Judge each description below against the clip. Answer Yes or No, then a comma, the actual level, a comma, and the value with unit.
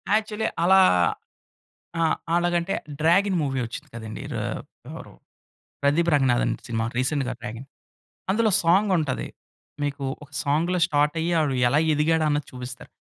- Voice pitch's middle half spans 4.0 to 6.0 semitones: Yes, average, 4.7 semitones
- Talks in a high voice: No, medium, 150 Hz